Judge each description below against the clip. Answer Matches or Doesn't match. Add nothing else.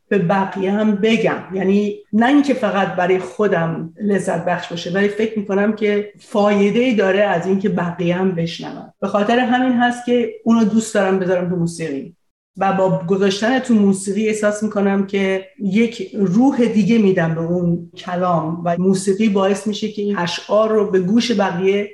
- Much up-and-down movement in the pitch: Doesn't match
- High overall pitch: Matches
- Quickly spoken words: Matches